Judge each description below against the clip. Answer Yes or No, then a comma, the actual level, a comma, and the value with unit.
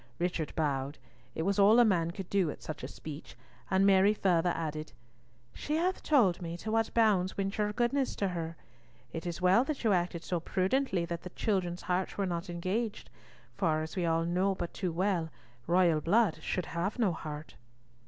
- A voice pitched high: No, medium, 180 Hz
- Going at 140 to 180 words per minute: No, average, 195 wpm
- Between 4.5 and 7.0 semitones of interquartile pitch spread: No, average, 3.3 semitones